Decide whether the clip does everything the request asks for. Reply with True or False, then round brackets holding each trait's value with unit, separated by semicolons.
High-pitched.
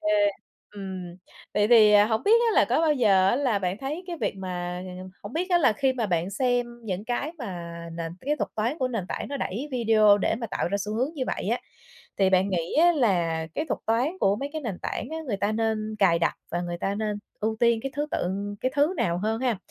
True (215 Hz)